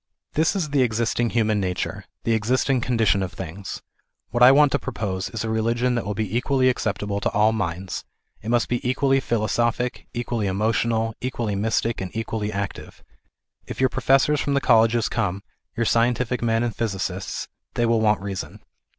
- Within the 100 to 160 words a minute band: No, average, 175 wpm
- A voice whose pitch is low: Yes, low, 115 Hz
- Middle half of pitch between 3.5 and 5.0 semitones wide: No, average, 2.9 semitones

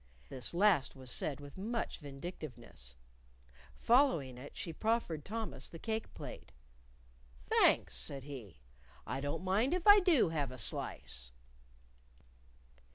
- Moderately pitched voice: Yes, medium, 155 Hz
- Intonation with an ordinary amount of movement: No, wide, 8.9 semitones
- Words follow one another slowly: Yes, slow, 125 wpm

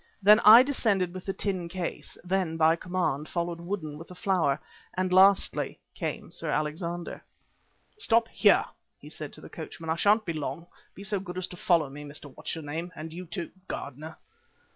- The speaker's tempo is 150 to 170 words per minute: No, average, 185 wpm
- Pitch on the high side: No, medium, 175 Hz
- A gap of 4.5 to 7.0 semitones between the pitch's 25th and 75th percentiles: No, average, 3.2 semitones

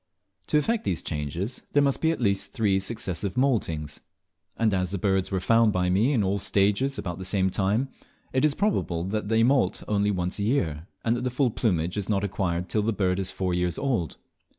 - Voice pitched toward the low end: Yes, low, 100 Hz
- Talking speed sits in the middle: No, fast, 220 wpm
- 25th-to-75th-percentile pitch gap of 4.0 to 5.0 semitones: Yes, average, 4.3 semitones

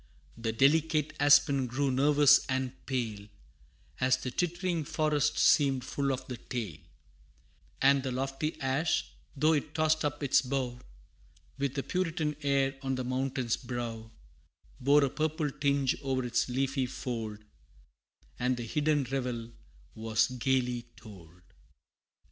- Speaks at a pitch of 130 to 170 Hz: Yes, low, 135 Hz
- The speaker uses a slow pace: Yes, slow, 130 wpm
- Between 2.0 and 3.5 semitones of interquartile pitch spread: Yes, average, 2.9 semitones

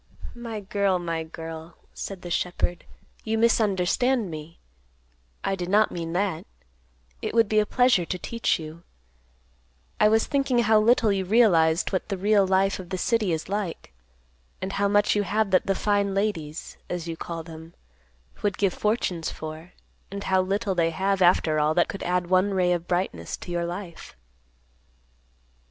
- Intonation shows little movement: No, average, 3.4 semitones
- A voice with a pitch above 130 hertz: Yes, high, 190 Hz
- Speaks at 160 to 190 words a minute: Yes, average, 170 wpm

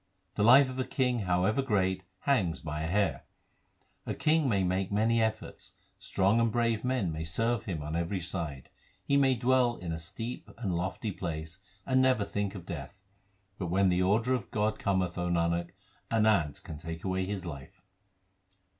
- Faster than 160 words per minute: Yes, average, 180 wpm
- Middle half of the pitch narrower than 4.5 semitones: No, average, 5.1 semitones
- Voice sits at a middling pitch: No, very low, 95 Hz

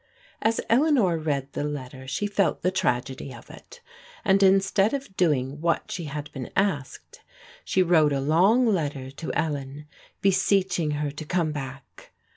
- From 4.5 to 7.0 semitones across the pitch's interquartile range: Yes, wide, 5.5 semitones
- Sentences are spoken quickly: No, average, 155 wpm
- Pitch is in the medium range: Yes, medium, 160 Hz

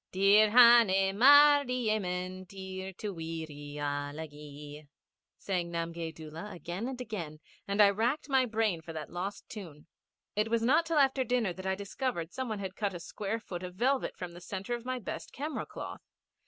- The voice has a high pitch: Yes, high, 195 Hz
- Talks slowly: No, average, 185 wpm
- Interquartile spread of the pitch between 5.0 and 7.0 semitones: Yes, wide, 5.6 semitones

